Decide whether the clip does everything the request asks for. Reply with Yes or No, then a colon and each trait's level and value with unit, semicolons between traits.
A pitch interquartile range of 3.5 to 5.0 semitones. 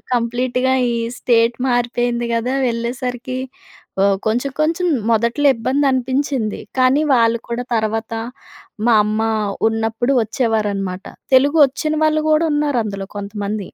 No: average, 2.8 semitones